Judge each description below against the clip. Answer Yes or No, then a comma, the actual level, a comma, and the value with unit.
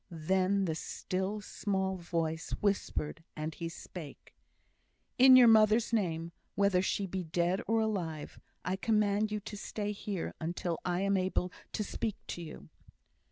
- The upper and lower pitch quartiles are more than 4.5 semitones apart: No, average, 3.5 semitones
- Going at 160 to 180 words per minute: No, average, 150 wpm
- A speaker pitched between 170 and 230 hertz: Yes, high, 190 Hz